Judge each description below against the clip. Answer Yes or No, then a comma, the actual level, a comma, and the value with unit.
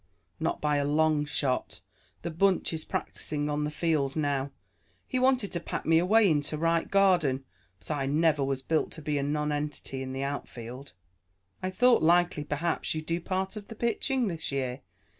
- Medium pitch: Yes, medium, 155 Hz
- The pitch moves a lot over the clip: No, average, 3.6 semitones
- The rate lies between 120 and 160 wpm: No, average, 180 wpm